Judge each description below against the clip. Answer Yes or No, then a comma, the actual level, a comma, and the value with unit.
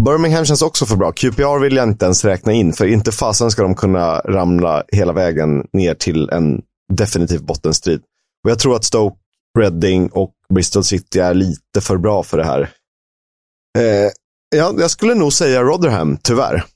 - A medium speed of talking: Yes, average, 180 wpm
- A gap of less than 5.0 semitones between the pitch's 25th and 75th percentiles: No, wide, 5.6 semitones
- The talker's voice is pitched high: No, low, 100 Hz